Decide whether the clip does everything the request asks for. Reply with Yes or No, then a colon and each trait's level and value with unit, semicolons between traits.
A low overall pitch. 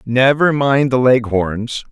Yes: low, 125 Hz